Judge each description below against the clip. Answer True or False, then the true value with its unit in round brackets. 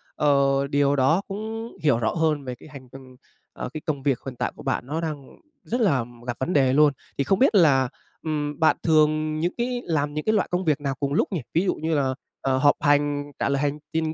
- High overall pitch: False (150 Hz)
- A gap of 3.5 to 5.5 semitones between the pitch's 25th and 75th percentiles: False (2.7 semitones)